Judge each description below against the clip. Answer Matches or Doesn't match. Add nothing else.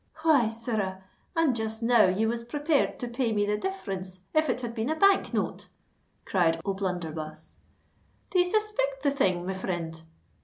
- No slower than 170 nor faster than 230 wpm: Doesn't match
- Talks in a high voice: Matches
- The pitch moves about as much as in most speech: Doesn't match